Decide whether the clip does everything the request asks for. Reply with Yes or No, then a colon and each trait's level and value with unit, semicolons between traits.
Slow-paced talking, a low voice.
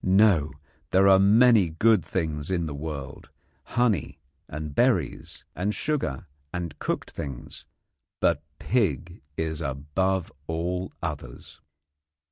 Yes: slow, 110 wpm; very low, 85 Hz